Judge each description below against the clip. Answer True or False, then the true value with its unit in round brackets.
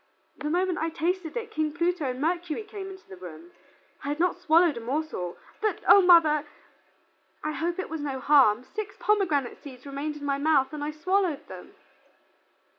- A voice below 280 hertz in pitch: False (310 Hz)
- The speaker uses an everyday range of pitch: True (4.3 semitones)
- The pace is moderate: True (185 wpm)